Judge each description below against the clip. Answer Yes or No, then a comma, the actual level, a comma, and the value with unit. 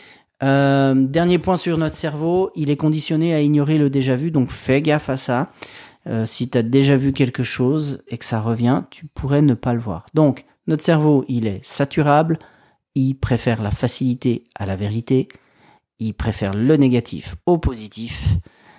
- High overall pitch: No, low, 135 Hz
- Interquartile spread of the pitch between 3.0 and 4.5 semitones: Yes, average, 3.9 semitones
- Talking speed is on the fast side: No, average, 180 wpm